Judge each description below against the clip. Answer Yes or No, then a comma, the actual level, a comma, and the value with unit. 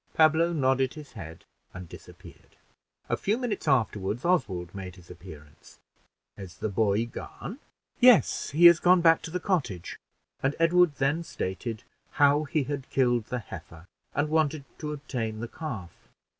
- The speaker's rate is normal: Yes, average, 155 wpm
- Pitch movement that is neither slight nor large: No, wide, 8.3 semitones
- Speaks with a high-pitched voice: No, low, 135 Hz